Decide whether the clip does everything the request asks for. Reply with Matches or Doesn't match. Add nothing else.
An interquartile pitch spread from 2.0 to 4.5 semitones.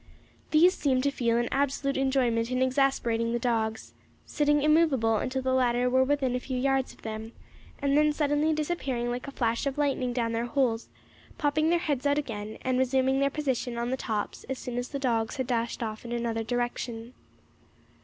Matches